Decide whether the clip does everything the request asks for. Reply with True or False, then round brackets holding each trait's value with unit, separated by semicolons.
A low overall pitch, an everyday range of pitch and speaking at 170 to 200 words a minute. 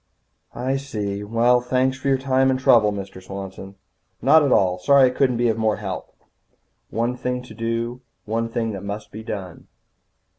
True (115 Hz; 3.7 semitones; 180 wpm)